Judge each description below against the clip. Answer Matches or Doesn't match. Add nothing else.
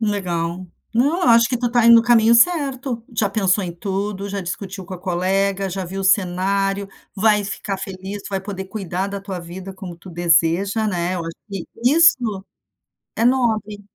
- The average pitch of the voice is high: Matches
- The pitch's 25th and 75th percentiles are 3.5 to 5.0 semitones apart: Doesn't match